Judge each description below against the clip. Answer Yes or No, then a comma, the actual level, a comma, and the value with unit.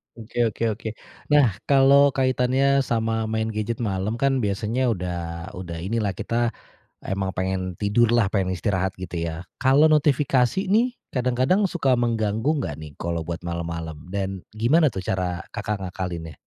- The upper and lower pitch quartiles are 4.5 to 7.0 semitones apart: Yes, wide, 5.6 semitones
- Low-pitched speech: Yes, low, 110 Hz